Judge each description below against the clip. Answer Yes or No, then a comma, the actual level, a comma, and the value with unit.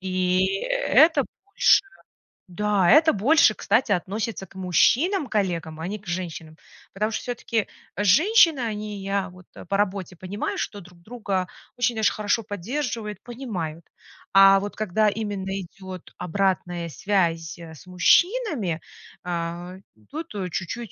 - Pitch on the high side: Yes, high, 195 Hz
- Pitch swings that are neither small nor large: Yes, average, 3.8 semitones